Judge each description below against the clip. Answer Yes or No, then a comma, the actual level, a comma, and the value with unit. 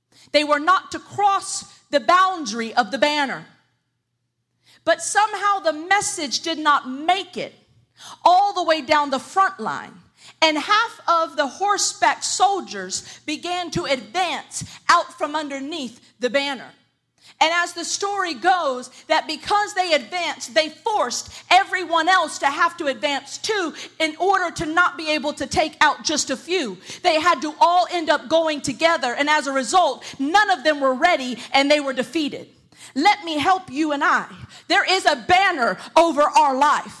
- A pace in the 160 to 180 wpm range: Yes, average, 165 wpm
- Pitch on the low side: No, very high, 320 Hz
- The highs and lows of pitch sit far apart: No, average, 4.4 semitones